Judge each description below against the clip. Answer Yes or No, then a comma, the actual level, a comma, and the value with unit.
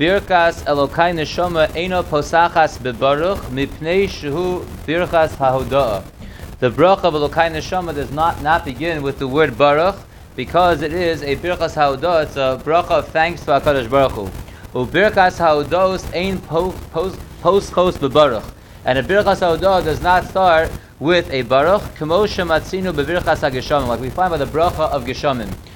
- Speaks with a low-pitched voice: No, medium, 155 Hz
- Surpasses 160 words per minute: No, average, 155 wpm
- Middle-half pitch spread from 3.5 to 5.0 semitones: Yes, average, 4.3 semitones